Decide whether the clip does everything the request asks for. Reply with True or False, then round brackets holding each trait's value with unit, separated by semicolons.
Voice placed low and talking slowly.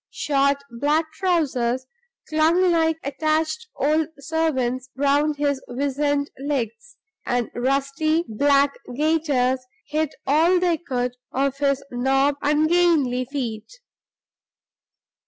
False (285 Hz; 100 wpm)